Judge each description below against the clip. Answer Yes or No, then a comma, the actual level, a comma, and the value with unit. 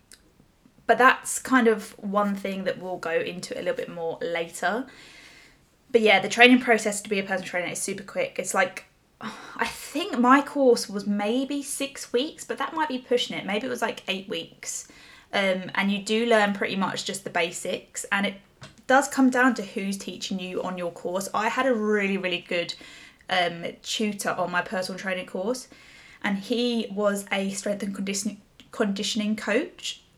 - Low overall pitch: No, high, 210 Hz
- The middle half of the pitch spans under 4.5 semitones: Yes, average, 4.1 semitones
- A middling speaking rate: Yes, average, 190 wpm